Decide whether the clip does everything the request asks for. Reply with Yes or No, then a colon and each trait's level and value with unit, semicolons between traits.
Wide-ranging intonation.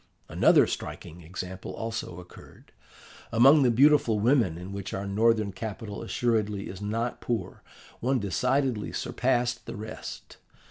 No: average, 3.5 semitones